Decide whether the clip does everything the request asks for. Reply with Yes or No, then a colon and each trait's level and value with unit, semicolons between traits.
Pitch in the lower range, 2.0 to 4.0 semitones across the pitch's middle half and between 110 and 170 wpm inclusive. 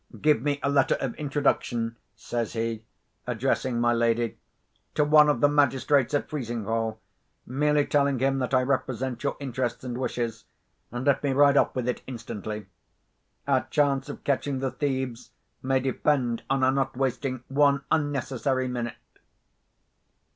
Yes: low, 130 Hz; average, 2.9 semitones; average, 145 wpm